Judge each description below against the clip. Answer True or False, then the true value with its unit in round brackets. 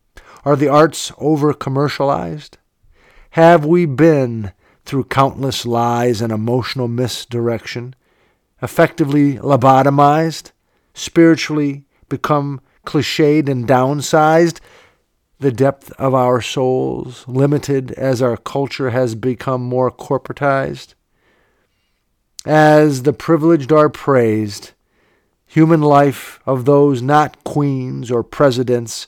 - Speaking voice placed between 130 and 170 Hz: True (135 Hz)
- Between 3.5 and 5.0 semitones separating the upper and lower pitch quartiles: False (3.1 semitones)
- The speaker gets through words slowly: True (95 wpm)